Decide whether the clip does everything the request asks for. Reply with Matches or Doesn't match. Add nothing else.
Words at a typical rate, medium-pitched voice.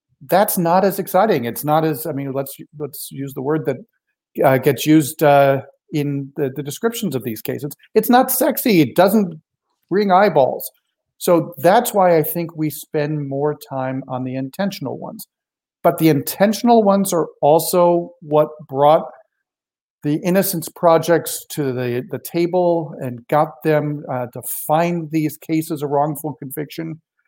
Matches